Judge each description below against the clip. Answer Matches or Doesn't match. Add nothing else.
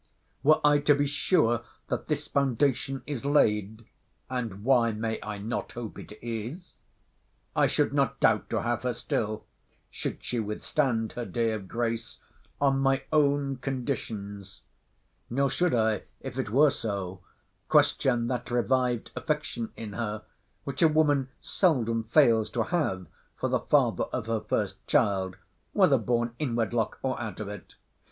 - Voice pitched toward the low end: Matches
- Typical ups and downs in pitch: Matches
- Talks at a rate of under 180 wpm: Matches